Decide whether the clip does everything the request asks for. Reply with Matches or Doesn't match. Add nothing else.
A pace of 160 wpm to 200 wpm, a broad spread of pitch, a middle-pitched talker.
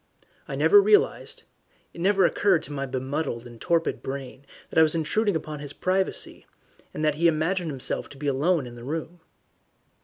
Doesn't match